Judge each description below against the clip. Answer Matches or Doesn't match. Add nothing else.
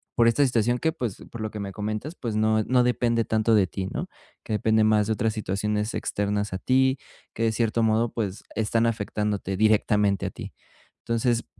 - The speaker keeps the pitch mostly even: Matches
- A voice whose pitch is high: Doesn't match